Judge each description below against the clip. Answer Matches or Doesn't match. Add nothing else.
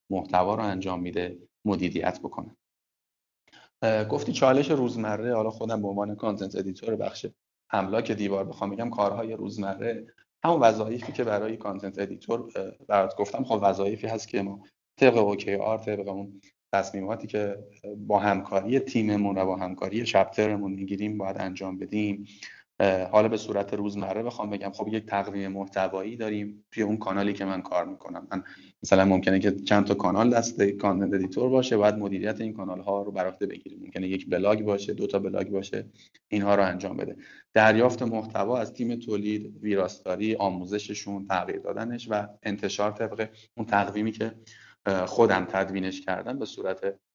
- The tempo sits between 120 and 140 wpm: Doesn't match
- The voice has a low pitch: Matches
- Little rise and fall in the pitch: Matches